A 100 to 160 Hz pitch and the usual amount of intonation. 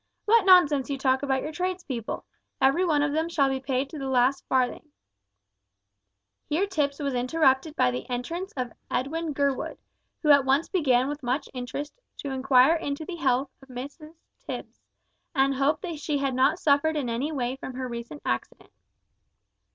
No: very high, 275 Hz; average, 3.2 semitones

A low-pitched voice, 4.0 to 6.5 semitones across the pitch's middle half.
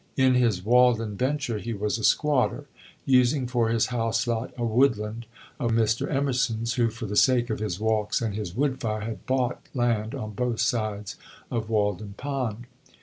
No: low, 115 Hz; narrow, 2.6 semitones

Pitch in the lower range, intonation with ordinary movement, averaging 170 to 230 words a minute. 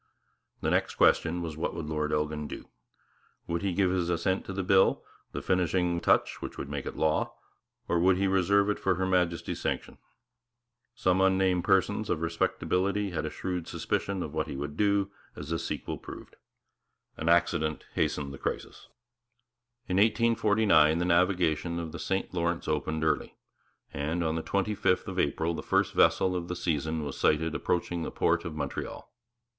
Yes: very low, 85 Hz; average, 3.2 semitones; average, 180 wpm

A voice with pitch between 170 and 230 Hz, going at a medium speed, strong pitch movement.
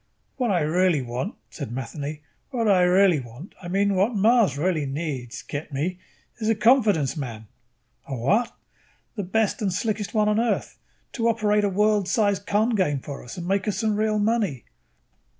Yes: high, 190 Hz; average, 180 wpm; wide, 6.3 semitones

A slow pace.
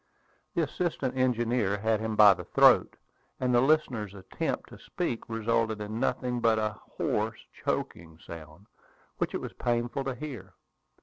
No: average, 150 wpm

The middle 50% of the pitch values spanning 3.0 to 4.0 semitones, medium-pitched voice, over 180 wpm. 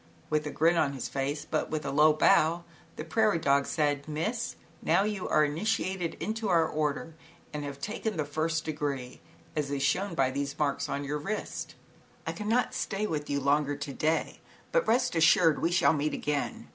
Yes: average, 3.4 semitones; medium, 155 Hz; average, 195 wpm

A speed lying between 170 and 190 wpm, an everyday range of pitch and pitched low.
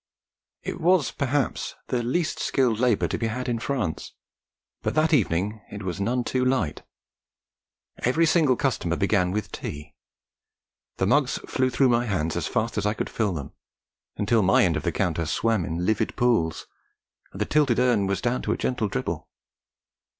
Yes: average, 175 wpm; average, 4.9 semitones; low, 115 Hz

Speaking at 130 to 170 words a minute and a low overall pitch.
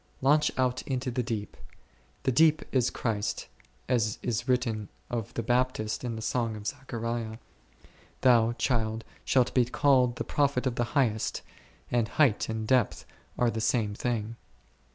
Yes: average, 155 wpm; low, 120 Hz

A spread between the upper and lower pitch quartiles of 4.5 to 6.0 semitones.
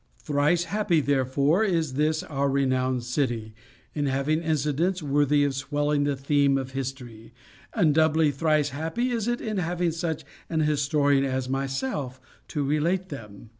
No: average, 2.9 semitones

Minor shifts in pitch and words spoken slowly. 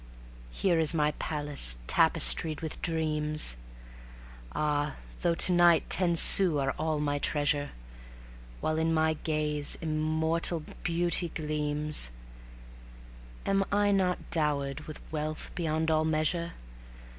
Yes: narrow, 1.9 semitones; slow, 115 wpm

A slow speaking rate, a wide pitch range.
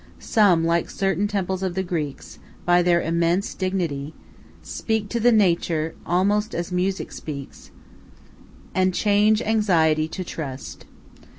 No: slow, 125 wpm; average, 3.4 semitones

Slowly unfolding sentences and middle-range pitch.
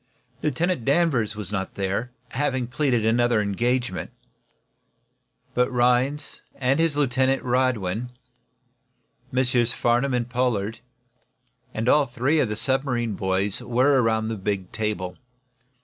No: slow, 115 wpm; low, 120 Hz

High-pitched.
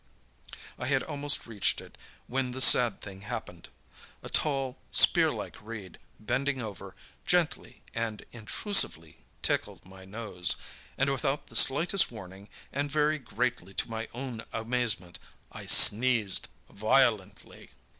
No: low, 120 Hz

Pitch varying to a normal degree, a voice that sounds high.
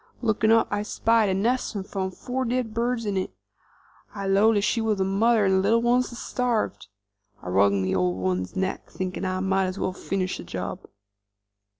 Yes: average, 3.4 semitones; high, 200 Hz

